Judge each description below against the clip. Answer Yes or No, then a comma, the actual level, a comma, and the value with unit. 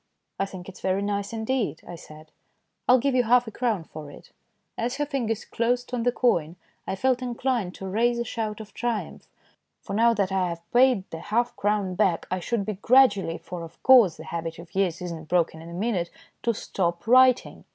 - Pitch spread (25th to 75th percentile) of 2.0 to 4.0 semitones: No, average, 5.3 semitones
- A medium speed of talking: No, fast, 215 wpm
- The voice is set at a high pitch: Yes, high, 205 Hz